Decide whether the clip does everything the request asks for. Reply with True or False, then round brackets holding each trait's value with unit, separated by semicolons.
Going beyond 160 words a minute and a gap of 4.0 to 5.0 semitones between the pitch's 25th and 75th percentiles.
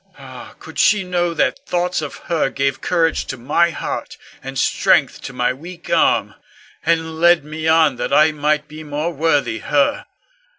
False (170 wpm; 2.8 semitones)